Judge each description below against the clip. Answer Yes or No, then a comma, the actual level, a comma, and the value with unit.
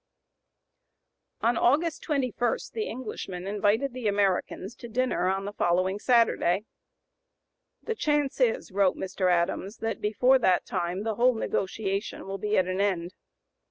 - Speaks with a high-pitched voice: Yes, high, 205 Hz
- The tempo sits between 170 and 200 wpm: No, average, 140 wpm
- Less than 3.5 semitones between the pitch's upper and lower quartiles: No, average, 4.5 semitones